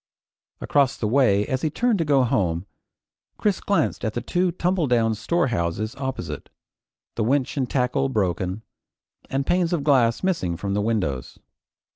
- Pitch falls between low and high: No, low, 125 Hz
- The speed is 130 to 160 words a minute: Yes, average, 150 wpm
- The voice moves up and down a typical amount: No, wide, 5.7 semitones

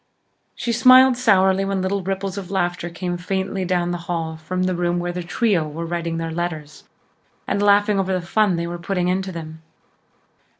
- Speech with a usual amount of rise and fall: No, narrow, 2.2 semitones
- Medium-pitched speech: Yes, medium, 180 Hz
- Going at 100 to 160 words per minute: No, average, 195 wpm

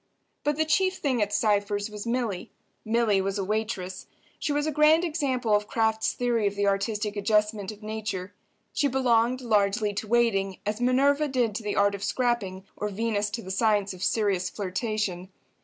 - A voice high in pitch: Yes, high, 215 Hz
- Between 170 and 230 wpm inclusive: Yes, average, 180 wpm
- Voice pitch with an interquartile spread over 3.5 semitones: No, average, 3.1 semitones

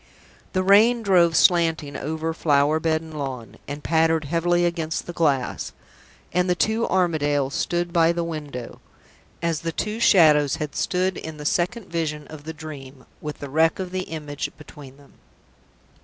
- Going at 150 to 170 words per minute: Yes, average, 165 wpm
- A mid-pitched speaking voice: Yes, medium, 160 Hz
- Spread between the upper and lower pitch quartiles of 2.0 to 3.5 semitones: Yes, average, 2.8 semitones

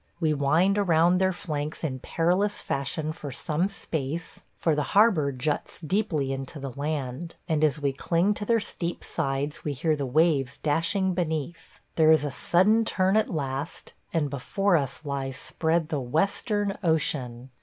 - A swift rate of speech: No, average, 165 wpm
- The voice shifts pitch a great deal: No, average, 4.0 semitones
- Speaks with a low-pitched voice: No, medium, 155 Hz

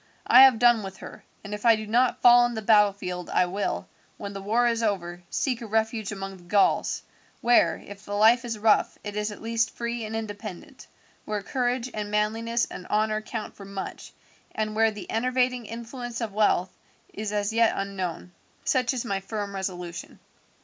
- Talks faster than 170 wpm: Yes, average, 190 wpm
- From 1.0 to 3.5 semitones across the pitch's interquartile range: Yes, narrow, 2.6 semitones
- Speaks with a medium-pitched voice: No, high, 215 Hz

